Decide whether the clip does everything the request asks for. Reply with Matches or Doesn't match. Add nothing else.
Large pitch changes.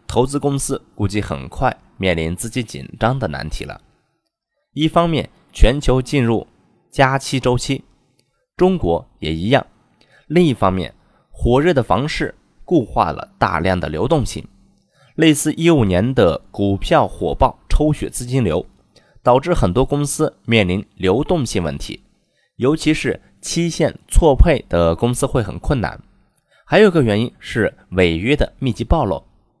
Matches